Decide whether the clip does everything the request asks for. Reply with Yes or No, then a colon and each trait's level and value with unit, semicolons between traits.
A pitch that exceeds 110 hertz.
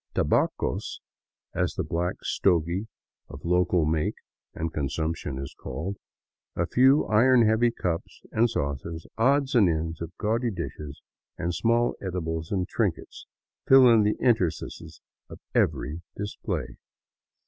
No: very low, 90 Hz